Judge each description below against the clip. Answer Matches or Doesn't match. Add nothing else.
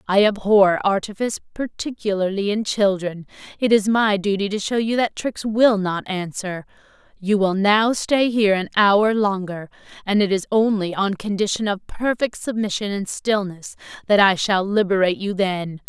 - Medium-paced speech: Matches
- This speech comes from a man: Doesn't match